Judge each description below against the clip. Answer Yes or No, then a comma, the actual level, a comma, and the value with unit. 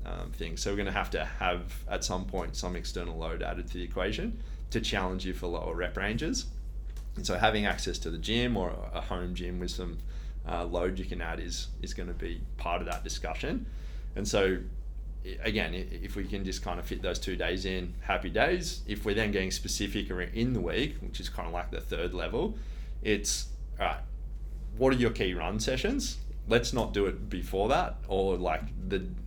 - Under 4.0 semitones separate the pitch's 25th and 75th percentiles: Yes, average, 2.7 semitones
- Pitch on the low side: Yes, very low, 90 Hz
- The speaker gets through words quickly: Yes, fast, 210 wpm